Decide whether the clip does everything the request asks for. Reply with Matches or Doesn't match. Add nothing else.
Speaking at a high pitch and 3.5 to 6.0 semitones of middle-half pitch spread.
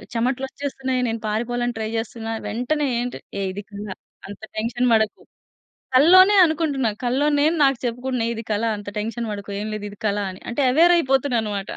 Matches